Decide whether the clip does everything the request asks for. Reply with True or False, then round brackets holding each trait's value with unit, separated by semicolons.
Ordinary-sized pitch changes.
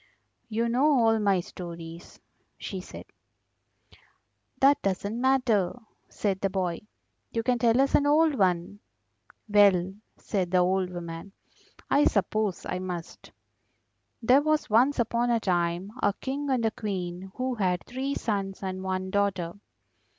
True (4.8 semitones)